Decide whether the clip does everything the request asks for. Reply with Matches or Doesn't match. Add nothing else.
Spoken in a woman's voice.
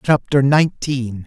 Doesn't match